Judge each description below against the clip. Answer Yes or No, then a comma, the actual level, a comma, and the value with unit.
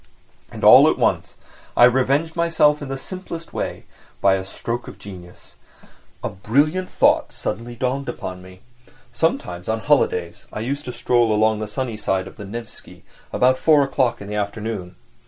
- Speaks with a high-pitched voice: No, low, 120 Hz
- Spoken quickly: No, average, 170 wpm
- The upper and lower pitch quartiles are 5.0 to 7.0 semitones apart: Yes, wide, 5.4 semitones